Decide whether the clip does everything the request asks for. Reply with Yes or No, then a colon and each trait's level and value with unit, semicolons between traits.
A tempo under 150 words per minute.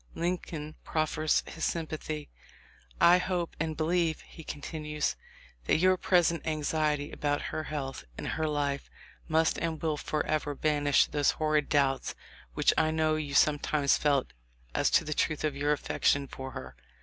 No: average, 160 wpm